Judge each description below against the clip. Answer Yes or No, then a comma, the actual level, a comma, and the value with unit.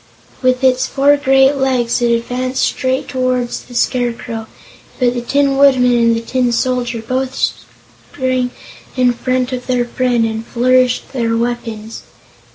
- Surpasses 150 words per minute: No, average, 145 wpm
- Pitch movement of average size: No, narrow, 1.4 semitones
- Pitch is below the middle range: No, very high, 250 Hz